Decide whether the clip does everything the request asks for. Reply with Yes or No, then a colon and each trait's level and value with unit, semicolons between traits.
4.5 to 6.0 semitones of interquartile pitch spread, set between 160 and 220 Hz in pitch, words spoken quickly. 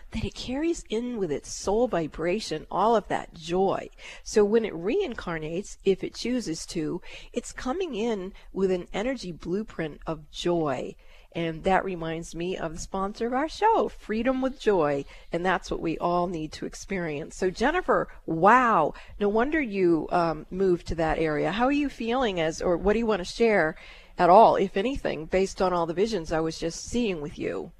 No: wide, 5.6 semitones; high, 190 Hz; average, 190 wpm